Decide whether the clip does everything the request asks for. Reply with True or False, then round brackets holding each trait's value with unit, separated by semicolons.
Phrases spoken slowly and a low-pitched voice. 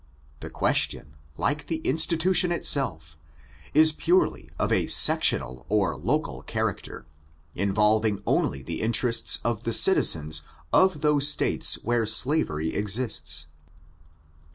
True (110 wpm; 115 Hz)